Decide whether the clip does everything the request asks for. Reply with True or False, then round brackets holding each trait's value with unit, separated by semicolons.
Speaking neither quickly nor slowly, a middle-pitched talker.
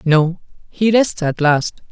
True (155 wpm; 175 Hz)